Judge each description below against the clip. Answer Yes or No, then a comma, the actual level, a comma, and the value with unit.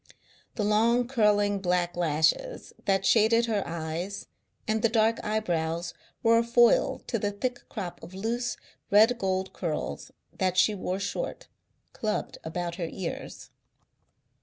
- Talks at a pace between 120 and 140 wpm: Yes, slow, 135 wpm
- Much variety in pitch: No, average, 4.3 semitones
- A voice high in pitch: Yes, high, 205 Hz